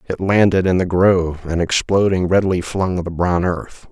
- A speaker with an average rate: Yes, average, 185 wpm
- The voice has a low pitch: Yes, very low, 90 Hz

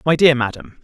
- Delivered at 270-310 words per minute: No, fast, 215 wpm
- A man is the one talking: Yes, male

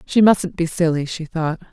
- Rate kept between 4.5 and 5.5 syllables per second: Yes, 4.6 syllables/s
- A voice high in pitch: No, medium, 165 Hz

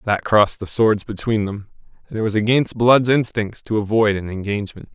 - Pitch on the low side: Yes, low, 110 Hz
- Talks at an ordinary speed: Yes, average, 195 wpm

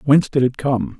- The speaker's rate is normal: No, fast, 240 wpm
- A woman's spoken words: No, male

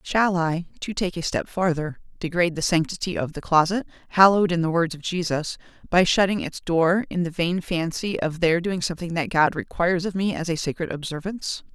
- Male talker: No, female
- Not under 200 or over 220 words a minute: Yes, fast, 205 wpm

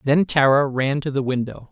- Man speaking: Yes, male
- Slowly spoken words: No, fast, 210 wpm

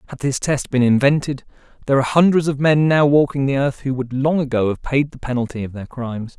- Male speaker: Yes, male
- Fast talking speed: Yes, fast, 235 wpm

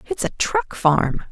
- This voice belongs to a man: No, female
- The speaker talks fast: No, average, 180 wpm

